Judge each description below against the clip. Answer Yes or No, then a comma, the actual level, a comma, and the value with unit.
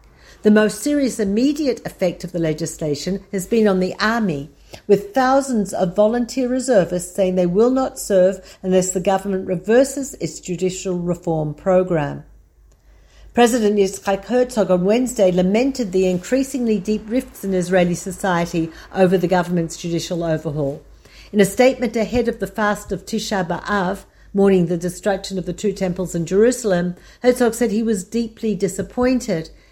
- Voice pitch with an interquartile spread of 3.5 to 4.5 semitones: Yes, average, 4.0 semitones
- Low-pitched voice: No, high, 195 Hz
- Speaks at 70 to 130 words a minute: No, fast, 150 wpm